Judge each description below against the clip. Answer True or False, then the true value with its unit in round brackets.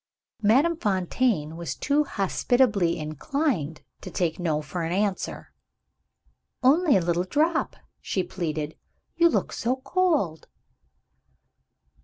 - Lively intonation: True (8.8 semitones)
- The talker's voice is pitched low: False (195 Hz)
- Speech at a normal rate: False (110 wpm)